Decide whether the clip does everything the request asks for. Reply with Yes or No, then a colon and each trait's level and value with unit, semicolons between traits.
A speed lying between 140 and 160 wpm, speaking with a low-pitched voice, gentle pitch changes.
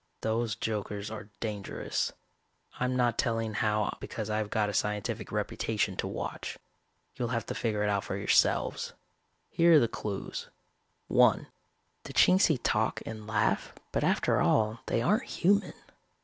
Yes: average, 150 wpm; low, 110 Hz; narrow, 2.1 semitones